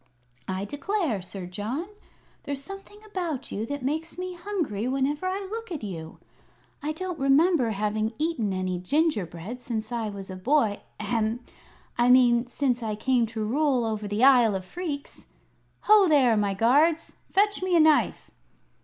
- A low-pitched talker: No, very high, 255 Hz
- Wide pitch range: Yes, wide, 7.1 semitones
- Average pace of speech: Yes, average, 160 wpm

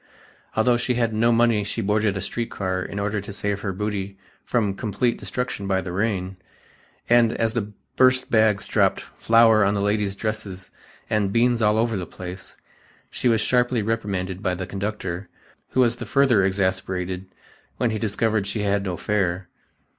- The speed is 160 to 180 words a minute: Yes, average, 175 wpm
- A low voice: Yes, low, 105 Hz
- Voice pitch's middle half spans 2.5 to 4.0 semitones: Yes, average, 2.9 semitones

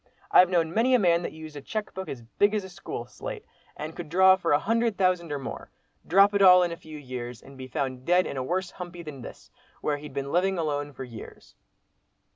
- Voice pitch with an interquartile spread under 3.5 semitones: No, average, 4.9 semitones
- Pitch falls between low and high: Yes, medium, 170 Hz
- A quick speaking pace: Yes, fast, 240 wpm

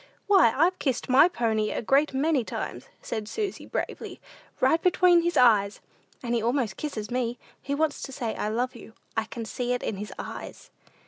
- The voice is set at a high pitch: Yes, very high, 250 Hz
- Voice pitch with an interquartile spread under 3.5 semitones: No, wide, 5.4 semitones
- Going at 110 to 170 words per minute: No, average, 190 wpm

